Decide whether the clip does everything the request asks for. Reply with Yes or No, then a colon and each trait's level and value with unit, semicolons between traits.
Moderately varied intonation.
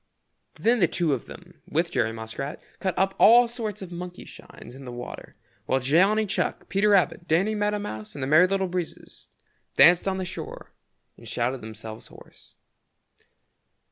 No: wide, 7.1 semitones